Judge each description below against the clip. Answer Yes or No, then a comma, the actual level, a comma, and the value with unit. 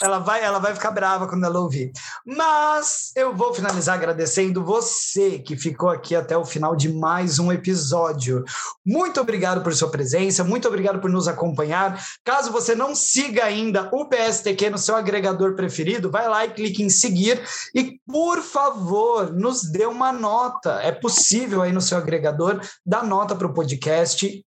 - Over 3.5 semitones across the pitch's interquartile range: Yes, average, 5.1 semitones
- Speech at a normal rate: Yes, average, 170 wpm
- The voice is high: Yes, high, 195 Hz